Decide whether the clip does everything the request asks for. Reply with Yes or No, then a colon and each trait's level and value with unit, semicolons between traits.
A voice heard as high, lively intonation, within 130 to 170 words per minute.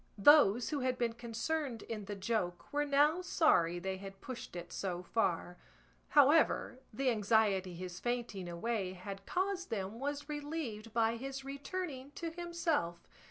Yes: high, 230 Hz; wide, 6.9 semitones; average, 150 wpm